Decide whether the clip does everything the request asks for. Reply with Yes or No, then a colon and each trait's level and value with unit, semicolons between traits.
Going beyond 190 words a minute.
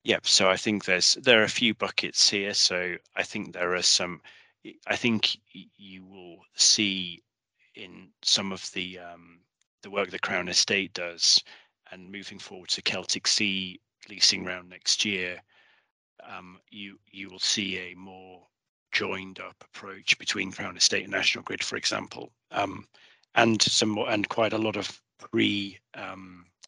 No: average, 160 wpm